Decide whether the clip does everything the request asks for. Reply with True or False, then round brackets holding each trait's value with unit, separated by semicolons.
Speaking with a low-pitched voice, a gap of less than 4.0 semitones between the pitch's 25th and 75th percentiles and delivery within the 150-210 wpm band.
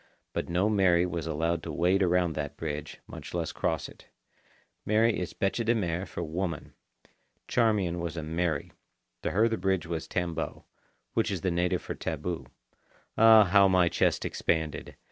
True (85 Hz; 2.9 semitones; 165 wpm)